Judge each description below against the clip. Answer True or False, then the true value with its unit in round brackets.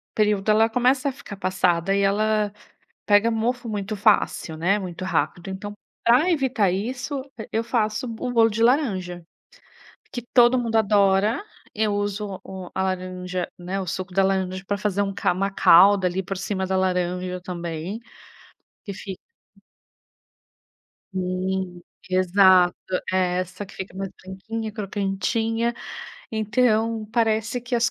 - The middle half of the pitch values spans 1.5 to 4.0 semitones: True (3.1 semitones)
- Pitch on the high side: True (200 Hz)